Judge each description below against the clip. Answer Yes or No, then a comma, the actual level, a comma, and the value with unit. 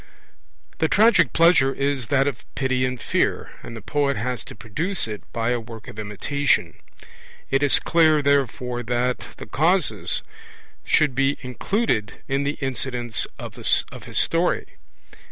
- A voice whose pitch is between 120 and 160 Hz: Yes, low, 135 Hz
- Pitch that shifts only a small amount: No, average, 3.1 semitones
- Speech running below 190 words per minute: Yes, average, 145 wpm